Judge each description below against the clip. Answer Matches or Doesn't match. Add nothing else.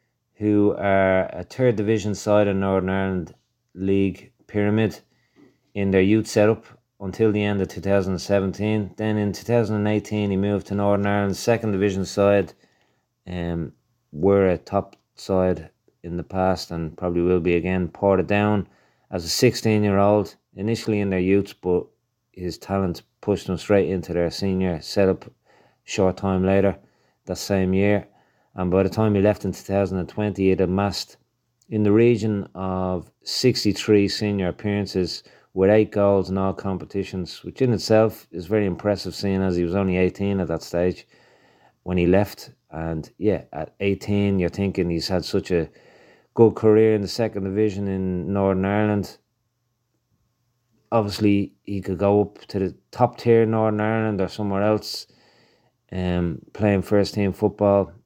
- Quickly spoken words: Doesn't match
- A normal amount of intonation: Doesn't match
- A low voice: Matches